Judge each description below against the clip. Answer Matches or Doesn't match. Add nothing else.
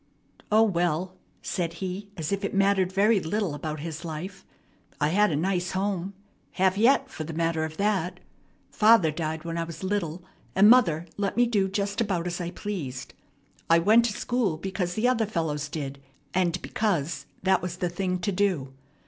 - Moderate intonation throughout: Matches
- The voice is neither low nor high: Matches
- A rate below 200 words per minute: Matches